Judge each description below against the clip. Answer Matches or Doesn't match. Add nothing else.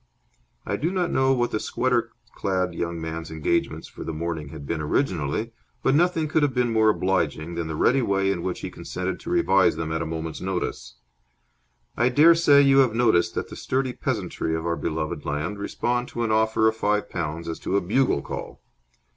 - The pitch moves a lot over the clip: Matches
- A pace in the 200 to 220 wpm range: Matches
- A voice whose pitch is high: Doesn't match